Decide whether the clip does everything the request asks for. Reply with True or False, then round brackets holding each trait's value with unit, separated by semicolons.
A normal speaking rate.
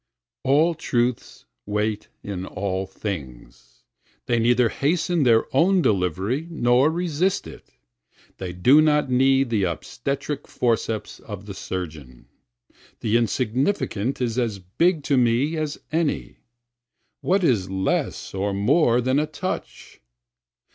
False (125 wpm)